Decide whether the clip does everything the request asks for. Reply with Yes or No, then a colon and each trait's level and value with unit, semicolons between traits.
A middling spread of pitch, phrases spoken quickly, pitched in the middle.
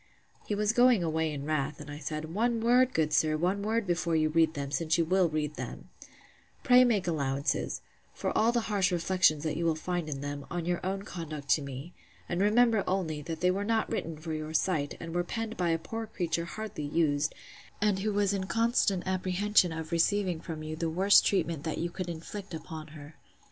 Yes: average, 4.4 semitones; fast, 210 wpm; medium, 170 Hz